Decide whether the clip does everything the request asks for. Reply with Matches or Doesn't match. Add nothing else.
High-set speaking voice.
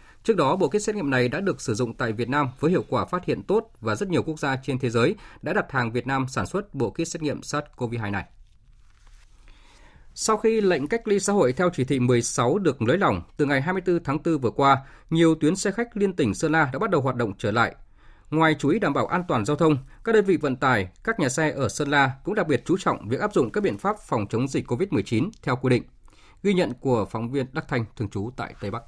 Doesn't match